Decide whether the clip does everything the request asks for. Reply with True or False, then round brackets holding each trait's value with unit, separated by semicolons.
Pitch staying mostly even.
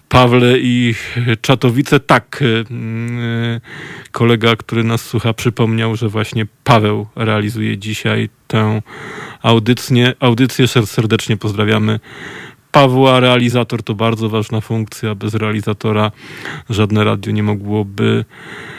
True (2.2 semitones)